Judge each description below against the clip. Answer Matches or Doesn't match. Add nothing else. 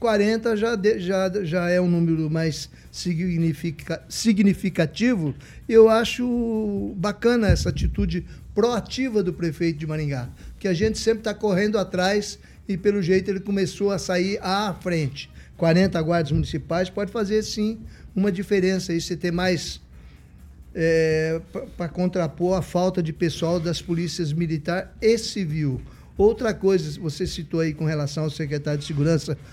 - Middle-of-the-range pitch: Matches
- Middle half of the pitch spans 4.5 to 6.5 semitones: Doesn't match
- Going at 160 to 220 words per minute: Doesn't match